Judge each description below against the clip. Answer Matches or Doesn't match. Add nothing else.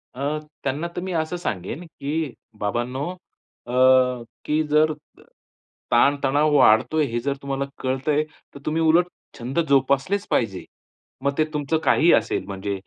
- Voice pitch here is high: Doesn't match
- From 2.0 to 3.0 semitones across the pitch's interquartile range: Doesn't match